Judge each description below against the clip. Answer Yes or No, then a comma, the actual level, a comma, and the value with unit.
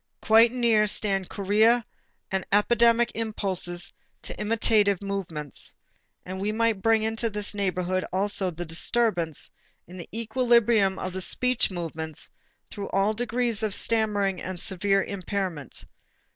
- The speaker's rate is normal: No, slow, 130 wpm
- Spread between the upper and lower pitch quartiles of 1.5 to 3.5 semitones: Yes, average, 3.2 semitones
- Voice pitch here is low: No, high, 205 Hz